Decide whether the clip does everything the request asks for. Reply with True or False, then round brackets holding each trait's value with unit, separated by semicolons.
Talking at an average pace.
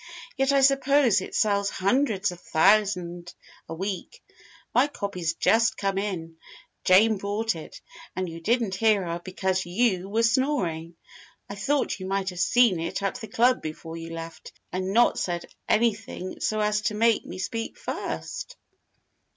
True (160 wpm)